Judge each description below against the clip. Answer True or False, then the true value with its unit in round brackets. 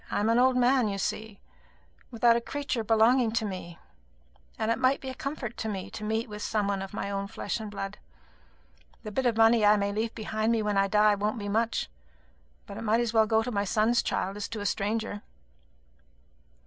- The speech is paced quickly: True (220 wpm)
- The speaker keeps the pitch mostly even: True (2.1 semitones)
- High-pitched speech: True (220 Hz)